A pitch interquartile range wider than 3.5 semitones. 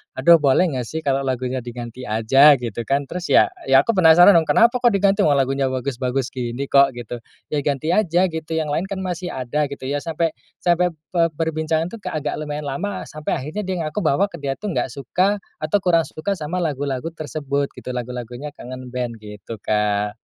Yes: average, 5.0 semitones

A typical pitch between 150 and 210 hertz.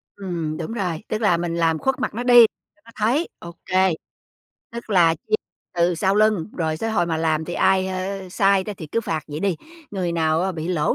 Yes: medium, 185 Hz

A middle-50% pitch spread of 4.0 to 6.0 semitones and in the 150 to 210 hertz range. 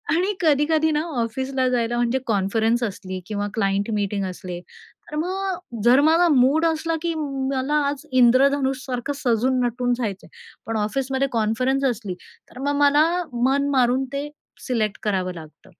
No: average, 4.3 semitones; very high, 255 Hz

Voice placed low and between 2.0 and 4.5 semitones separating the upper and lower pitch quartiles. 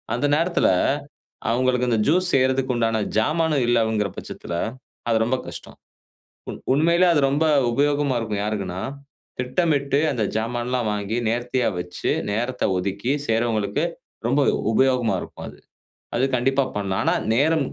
Yes: low, 125 Hz; average, 4.0 semitones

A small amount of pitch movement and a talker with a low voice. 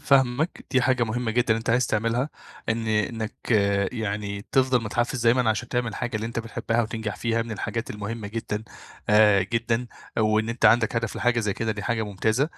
Yes: narrow, 1.9 semitones; low, 115 Hz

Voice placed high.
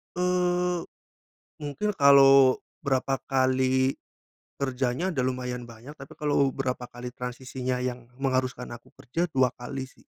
No: low, 130 Hz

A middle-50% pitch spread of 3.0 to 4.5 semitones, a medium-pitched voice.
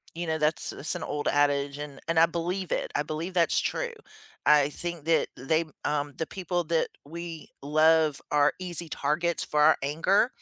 No: narrow, 2.6 semitones; medium, 160 Hz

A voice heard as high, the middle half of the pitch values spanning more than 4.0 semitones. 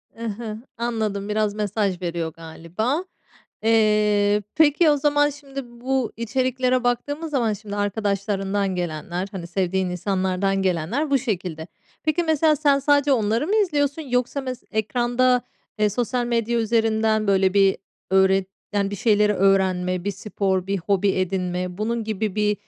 Yes: high, 215 Hz; average, 4.6 semitones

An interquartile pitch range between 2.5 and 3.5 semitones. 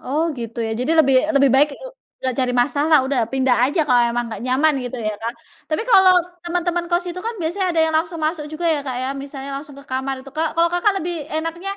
No: average, 4.4 semitones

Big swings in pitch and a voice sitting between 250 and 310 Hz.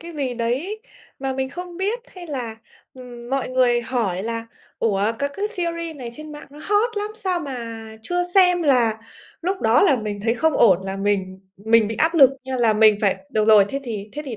Yes: wide, 7.1 semitones; very high, 255 Hz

